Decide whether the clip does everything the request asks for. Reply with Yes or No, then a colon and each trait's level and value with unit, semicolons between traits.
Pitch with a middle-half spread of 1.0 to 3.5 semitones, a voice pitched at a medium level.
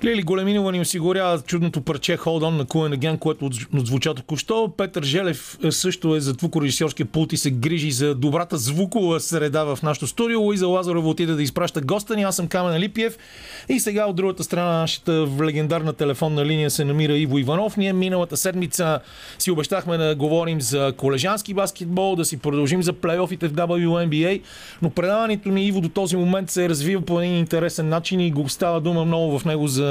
Yes: average, 3.1 semitones; medium, 170 Hz